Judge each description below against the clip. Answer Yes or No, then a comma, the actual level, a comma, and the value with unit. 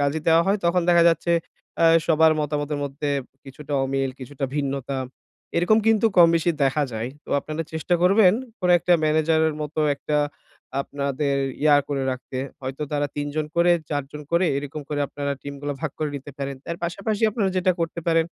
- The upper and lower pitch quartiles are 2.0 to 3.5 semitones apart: Yes, average, 3.1 semitones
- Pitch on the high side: No, medium, 150 Hz